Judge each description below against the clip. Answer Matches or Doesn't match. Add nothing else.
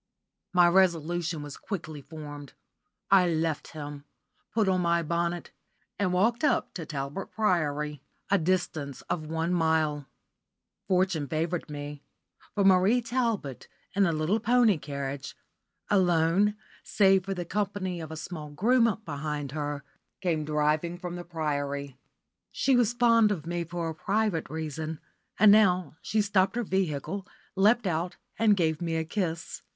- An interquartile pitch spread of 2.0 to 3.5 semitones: Doesn't match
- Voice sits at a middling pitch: Matches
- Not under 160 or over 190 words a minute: Doesn't match